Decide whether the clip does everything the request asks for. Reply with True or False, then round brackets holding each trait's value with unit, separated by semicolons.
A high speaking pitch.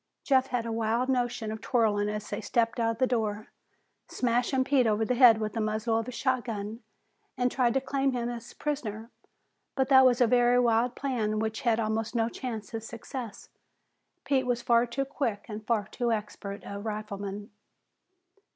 True (230 Hz)